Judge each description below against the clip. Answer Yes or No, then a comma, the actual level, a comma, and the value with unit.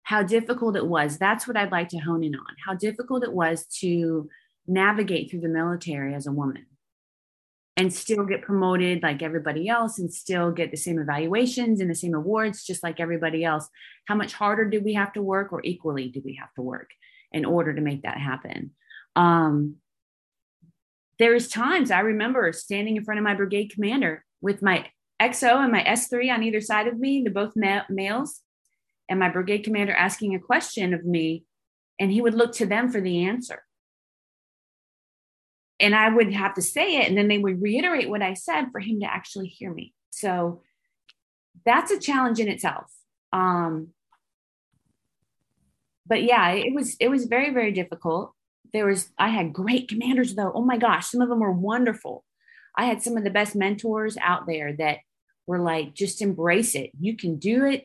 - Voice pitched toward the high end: Yes, high, 200 Hz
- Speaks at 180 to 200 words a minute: Yes, average, 190 wpm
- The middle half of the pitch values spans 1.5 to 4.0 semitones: No, average, 5.1 semitones